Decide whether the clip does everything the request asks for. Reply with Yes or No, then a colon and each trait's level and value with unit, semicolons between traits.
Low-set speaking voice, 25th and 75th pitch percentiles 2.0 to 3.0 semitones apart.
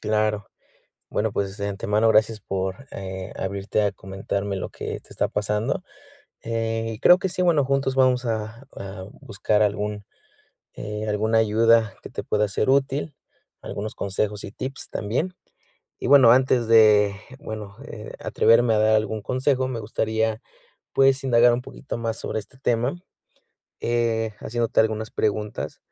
Yes: low, 110 Hz; narrow, 2.6 semitones